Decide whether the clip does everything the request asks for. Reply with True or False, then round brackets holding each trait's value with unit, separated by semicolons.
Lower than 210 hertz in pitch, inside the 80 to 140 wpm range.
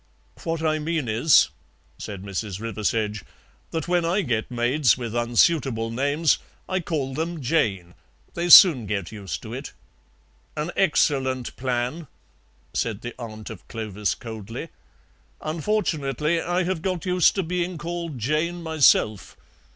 True (135 Hz; 135 wpm)